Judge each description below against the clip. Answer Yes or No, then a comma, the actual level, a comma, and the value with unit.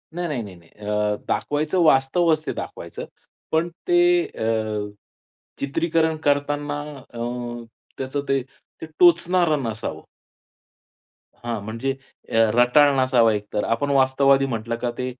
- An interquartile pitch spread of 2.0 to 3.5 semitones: No, average, 5.2 semitones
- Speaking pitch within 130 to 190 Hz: Yes, low, 135 Hz